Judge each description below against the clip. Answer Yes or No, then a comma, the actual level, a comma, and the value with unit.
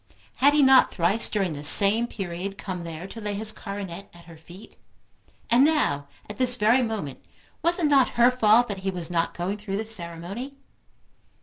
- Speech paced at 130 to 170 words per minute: No, average, 190 wpm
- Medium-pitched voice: No, high, 205 Hz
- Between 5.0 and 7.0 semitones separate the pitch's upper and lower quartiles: Yes, wide, 5.4 semitones